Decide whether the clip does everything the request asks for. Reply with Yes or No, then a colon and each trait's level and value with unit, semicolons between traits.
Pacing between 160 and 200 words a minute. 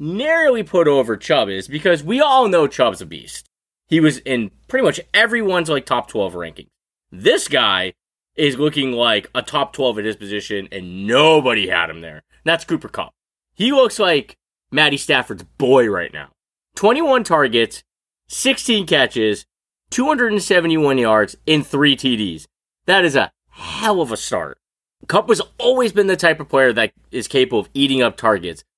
Yes: average, 165 wpm